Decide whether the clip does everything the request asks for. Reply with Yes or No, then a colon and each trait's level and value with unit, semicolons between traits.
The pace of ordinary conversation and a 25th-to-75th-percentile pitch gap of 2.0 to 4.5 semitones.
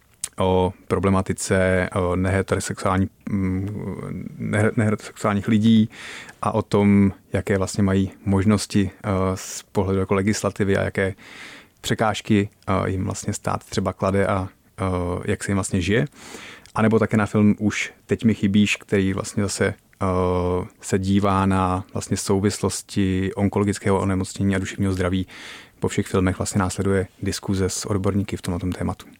No: average, 130 wpm; narrow, 1.5 semitones